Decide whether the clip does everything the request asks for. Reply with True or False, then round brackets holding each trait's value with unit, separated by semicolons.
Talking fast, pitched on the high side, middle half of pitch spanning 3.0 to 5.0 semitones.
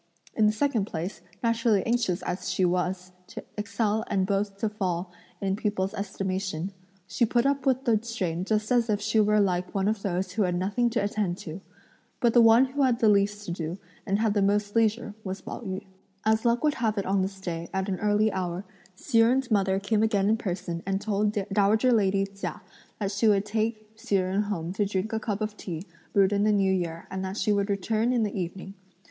False (220 wpm; 205 Hz; 2.5 semitones)